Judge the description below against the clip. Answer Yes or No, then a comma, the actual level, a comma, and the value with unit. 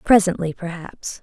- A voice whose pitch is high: No, medium, 180 Hz